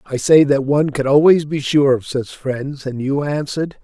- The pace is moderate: No, fast, 220 wpm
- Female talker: No, male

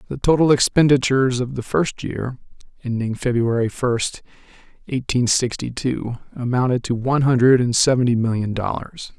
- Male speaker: Yes, male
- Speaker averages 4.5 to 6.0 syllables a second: Yes, 5.1 syllables/s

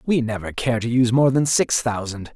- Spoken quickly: Yes, fast, 230 wpm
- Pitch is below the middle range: Yes, low, 120 Hz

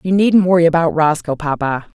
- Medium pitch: Yes, medium, 165 Hz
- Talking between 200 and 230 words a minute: No, average, 180 wpm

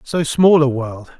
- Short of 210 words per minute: Yes, average, 200 wpm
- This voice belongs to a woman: No, male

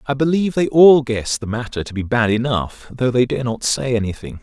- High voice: No, low, 125 Hz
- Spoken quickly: Yes, fast, 245 wpm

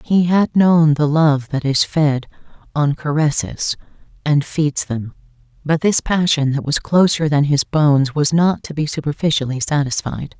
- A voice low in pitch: No, medium, 150 Hz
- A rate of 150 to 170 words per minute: Yes, average, 160 wpm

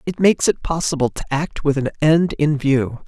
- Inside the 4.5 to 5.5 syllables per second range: Yes, 5.2 syllables/s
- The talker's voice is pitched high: No, medium, 145 Hz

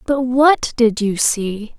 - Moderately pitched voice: No, high, 240 Hz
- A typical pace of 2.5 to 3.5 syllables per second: Yes, 3.1 syllables/s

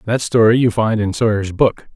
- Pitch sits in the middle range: No, low, 110 Hz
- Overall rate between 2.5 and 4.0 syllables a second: No, 5.1 syllables/s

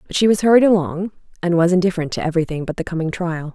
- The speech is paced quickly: Yes, fast, 235 wpm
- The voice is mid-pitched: Yes, medium, 175 Hz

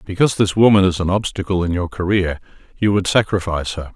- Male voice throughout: Yes, male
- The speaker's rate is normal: Yes, average, 195 wpm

